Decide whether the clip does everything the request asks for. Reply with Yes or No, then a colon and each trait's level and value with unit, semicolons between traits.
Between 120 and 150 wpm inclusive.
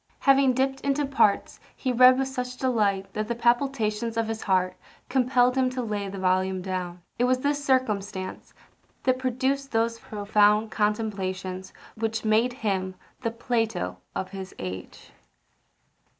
Yes: average, 145 wpm